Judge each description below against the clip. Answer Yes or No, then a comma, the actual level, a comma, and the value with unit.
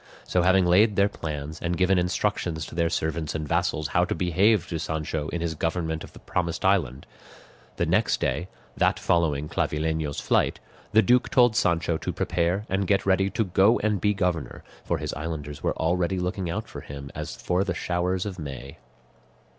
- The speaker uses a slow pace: No, average, 185 wpm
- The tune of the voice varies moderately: Yes, average, 3.2 semitones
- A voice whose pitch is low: Yes, very low, 85 Hz